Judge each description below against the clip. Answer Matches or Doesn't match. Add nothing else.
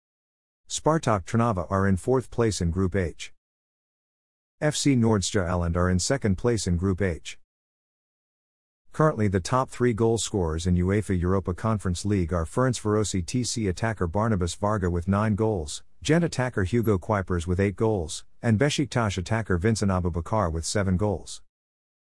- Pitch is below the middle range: Matches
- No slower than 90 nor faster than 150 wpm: Matches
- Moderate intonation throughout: Matches